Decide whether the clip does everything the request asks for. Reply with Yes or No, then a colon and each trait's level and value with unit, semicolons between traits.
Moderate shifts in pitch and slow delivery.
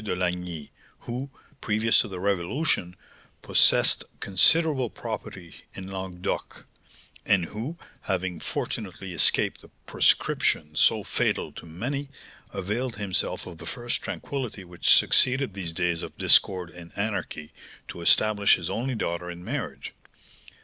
Yes: average, 4.7 semitones; slow, 130 wpm